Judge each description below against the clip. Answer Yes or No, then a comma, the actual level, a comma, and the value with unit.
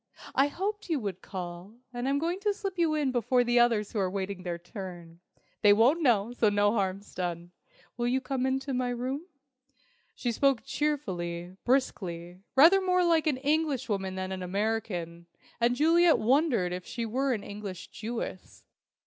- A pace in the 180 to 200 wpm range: No, average, 170 wpm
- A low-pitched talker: No, high, 235 Hz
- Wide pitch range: Yes, wide, 6.7 semitones